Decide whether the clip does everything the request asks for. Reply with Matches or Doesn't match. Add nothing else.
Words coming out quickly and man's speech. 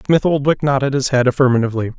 Doesn't match